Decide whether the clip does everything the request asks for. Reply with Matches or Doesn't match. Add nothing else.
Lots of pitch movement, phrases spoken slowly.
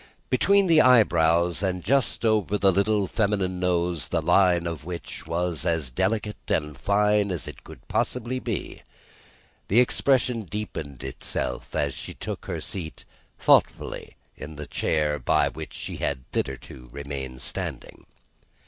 Doesn't match